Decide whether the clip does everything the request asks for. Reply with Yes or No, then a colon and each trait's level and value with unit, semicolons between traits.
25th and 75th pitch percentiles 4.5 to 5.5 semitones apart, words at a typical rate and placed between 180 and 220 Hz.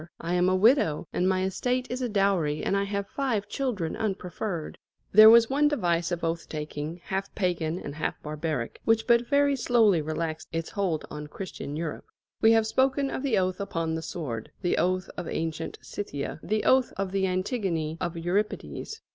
Yes: average, 5.1 semitones; average, 185 wpm; medium, 185 Hz